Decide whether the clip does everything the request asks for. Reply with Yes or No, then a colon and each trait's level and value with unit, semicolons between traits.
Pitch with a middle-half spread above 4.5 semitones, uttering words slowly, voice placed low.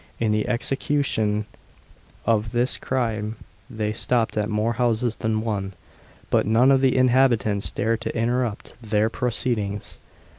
No: narrow, 2.5 semitones; slow, 125 wpm; low, 115 Hz